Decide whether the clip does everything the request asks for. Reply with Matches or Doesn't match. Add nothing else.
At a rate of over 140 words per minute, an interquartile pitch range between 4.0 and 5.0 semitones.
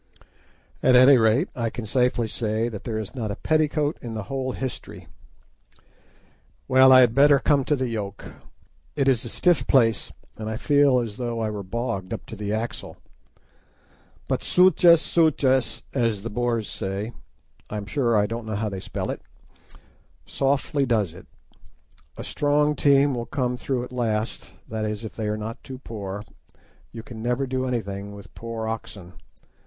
Doesn't match